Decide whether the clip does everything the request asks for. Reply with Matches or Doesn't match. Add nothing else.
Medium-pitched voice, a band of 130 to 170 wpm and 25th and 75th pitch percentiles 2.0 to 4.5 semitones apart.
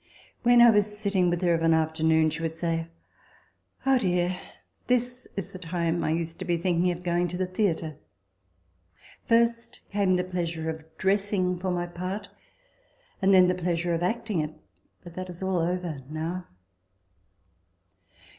Matches